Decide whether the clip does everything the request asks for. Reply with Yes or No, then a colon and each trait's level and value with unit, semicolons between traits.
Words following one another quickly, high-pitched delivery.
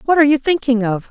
Yes: fast, 270 wpm; very high, 265 Hz